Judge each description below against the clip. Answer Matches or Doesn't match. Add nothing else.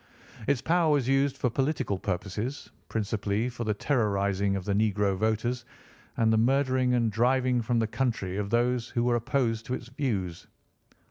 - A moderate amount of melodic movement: Matches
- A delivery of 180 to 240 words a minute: Doesn't match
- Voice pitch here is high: Doesn't match